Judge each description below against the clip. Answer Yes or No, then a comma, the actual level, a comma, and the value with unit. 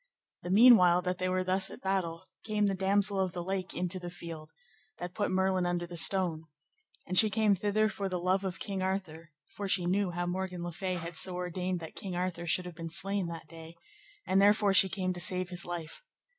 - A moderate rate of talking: No, fast, 220 wpm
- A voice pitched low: No, medium, 185 Hz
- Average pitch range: No, narrow, 1.7 semitones